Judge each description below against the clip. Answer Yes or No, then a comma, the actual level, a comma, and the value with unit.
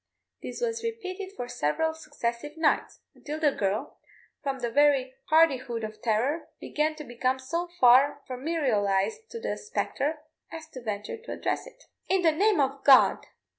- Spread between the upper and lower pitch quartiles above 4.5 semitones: Yes, average, 5.2 semitones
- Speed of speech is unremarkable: Yes, average, 160 wpm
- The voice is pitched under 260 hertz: No, very high, 290 Hz